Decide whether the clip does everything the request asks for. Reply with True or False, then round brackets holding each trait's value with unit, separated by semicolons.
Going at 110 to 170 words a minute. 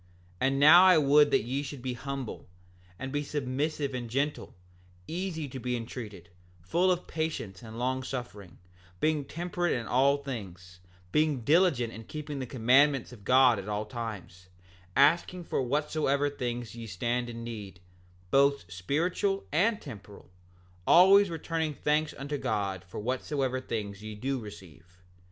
True (150 wpm)